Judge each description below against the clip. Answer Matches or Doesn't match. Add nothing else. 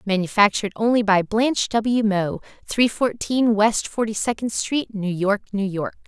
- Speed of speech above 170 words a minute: Doesn't match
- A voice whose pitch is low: Doesn't match